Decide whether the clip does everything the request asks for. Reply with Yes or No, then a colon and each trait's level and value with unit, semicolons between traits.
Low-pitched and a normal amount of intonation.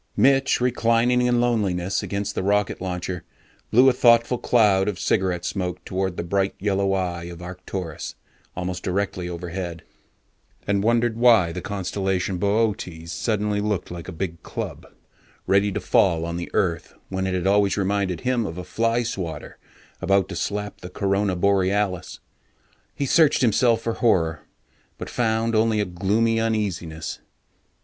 Yes: low, 100 Hz; average, 3.8 semitones